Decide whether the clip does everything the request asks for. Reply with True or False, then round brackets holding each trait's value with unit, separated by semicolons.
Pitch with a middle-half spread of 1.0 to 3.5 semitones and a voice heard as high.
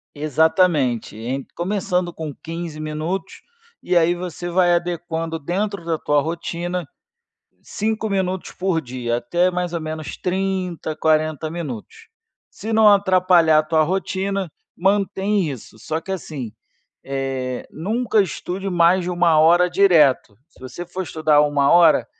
False (3.2 semitones; 170 Hz)